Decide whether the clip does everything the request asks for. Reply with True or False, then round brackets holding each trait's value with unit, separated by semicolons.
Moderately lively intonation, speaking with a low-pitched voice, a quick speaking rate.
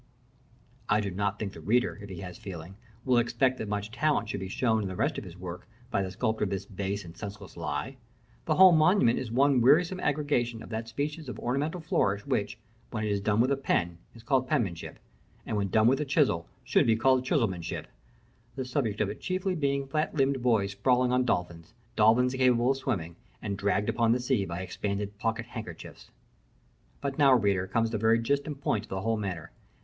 True (4.8 semitones; 115 Hz; 210 wpm)